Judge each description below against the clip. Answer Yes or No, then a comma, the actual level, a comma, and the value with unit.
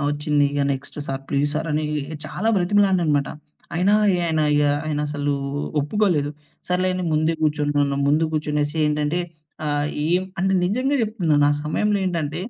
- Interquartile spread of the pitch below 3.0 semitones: No, average, 3.5 semitones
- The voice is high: No, medium, 155 Hz